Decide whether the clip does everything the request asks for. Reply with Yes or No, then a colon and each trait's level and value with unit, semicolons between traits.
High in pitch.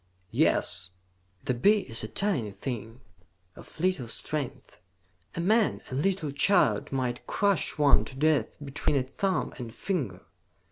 No: medium, 140 Hz